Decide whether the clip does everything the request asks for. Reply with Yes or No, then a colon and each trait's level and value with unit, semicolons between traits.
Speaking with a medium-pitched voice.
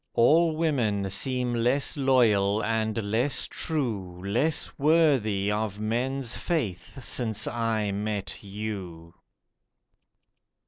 No: low, 115 Hz